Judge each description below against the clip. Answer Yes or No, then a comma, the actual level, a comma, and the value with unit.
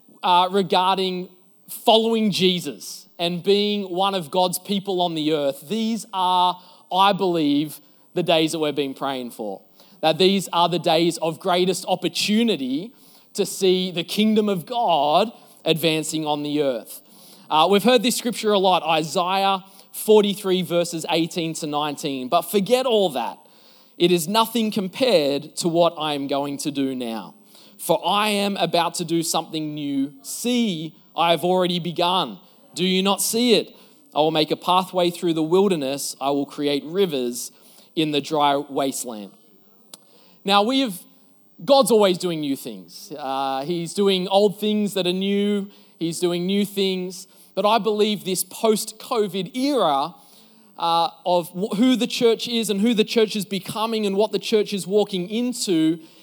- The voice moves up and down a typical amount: Yes, average, 4.2 semitones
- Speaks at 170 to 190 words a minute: No, average, 160 wpm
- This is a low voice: No, medium, 185 Hz